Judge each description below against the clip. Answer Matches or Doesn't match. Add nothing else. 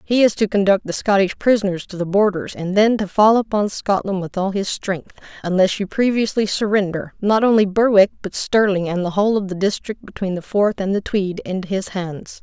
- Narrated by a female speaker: Matches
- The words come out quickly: Matches